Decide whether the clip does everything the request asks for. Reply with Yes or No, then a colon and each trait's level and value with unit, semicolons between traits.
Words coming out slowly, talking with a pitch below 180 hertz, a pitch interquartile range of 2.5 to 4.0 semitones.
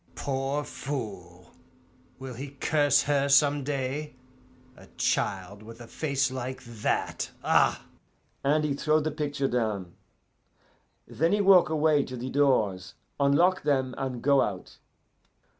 Yes: slow, 130 wpm; low, 135 Hz; average, 3.3 semitones